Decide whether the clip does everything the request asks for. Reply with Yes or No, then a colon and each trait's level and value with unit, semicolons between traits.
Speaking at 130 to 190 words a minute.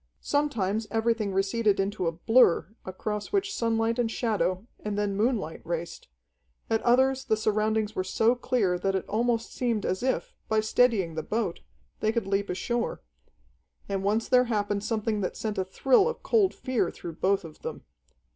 Yes: average, 170 wpm